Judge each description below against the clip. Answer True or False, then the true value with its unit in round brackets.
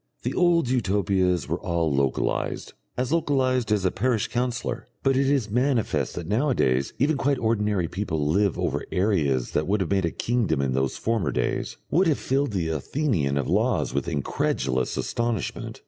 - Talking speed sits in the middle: True (175 wpm)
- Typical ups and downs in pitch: False (8.1 semitones)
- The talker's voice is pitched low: True (105 Hz)